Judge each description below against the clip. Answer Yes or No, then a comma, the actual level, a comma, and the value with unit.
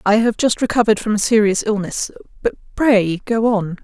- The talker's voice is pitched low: No, high, 210 Hz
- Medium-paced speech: Yes, average, 170 wpm